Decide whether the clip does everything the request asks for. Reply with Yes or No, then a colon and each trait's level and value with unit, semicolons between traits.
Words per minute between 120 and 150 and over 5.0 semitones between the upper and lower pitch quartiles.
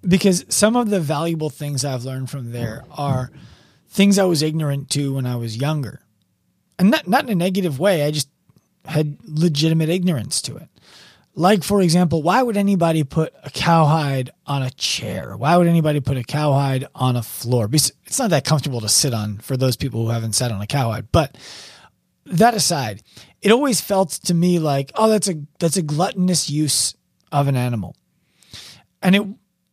No: average, 190 wpm; wide, 5.5 semitones